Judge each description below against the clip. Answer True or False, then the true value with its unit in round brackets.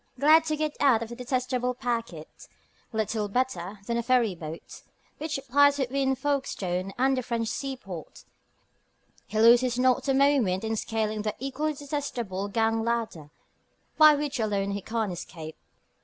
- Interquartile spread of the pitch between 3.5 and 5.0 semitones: True (4.4 semitones)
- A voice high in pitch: True (235 Hz)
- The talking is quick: False (150 wpm)